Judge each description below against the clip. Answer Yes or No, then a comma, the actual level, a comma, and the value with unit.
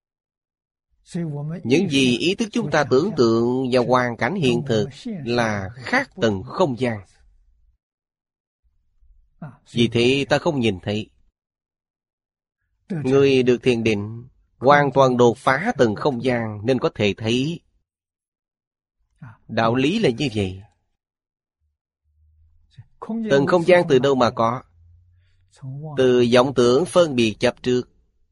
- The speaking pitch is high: No, low, 120 Hz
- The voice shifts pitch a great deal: Yes, wide, 6.5 semitones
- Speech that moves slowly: Yes, slow, 125 wpm